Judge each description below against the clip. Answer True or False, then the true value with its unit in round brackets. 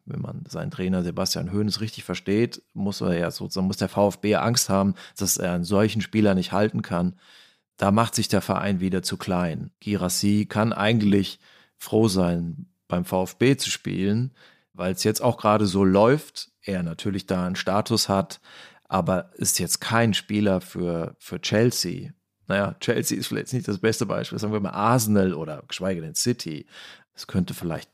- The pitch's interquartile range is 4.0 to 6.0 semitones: False (2.8 semitones)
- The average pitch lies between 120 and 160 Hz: False (100 Hz)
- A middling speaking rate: True (175 wpm)